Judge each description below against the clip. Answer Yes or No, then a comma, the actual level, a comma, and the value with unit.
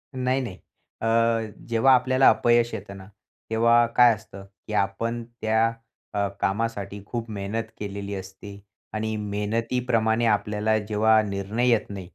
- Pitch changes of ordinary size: No, narrow, 2.3 semitones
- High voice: No, low, 110 Hz